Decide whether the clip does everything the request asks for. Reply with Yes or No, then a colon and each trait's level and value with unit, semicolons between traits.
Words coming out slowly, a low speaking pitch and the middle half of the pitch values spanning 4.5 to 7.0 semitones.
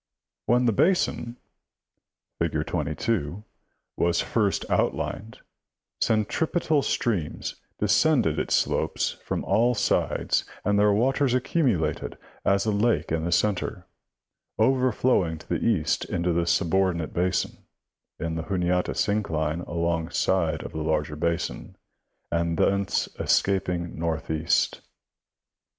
Yes: slow, 120 wpm; very low, 90 Hz; average, 4.8 semitones